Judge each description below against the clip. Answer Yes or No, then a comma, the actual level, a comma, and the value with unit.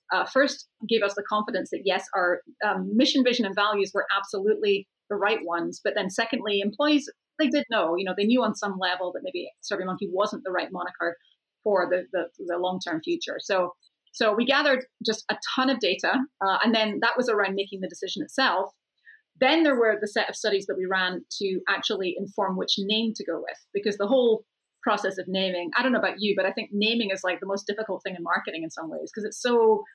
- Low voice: No, high, 205 Hz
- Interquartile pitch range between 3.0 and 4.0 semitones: Yes, average, 3.7 semitones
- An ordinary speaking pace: No, fast, 220 wpm